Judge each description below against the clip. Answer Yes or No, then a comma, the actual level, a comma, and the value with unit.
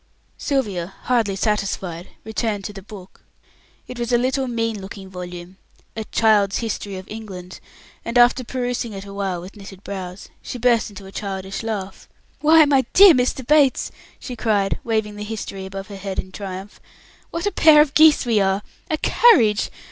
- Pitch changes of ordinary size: Yes, average, 4.1 semitones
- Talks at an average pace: Yes, average, 170 wpm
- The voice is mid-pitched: No, high, 210 Hz